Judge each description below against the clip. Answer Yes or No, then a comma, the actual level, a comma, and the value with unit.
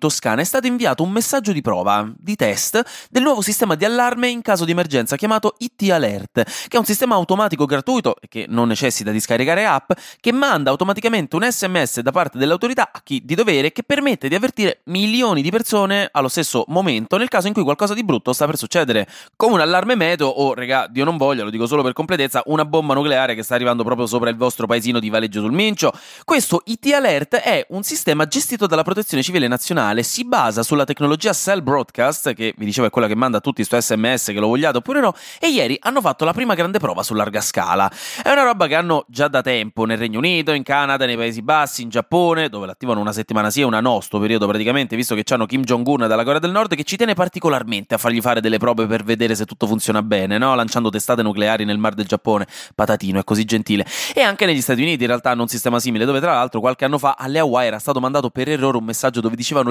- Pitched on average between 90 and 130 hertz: No, medium, 140 Hz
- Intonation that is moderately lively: No, wide, 8.1 semitones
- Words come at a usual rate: No, fast, 235 wpm